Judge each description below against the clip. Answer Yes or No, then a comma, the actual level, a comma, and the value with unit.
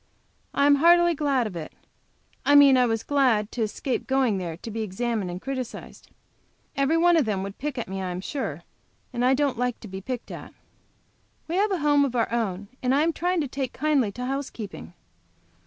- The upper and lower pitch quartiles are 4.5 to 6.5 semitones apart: Yes, average, 5.2 semitones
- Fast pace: Yes, fast, 210 wpm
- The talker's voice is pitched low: No, very high, 250 Hz